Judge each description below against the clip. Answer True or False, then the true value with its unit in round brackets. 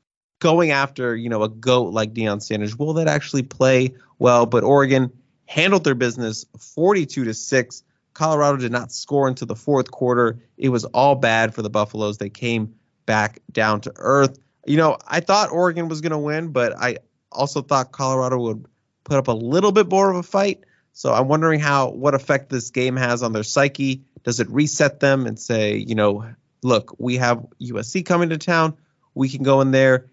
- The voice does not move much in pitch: False (3.7 semitones)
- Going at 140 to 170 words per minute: False (195 wpm)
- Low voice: True (130 Hz)